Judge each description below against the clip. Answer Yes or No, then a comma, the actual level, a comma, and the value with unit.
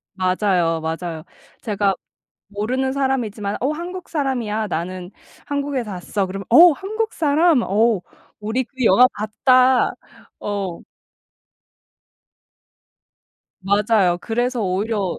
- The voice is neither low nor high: No, high, 215 Hz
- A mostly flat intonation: No, wide, 5.4 semitones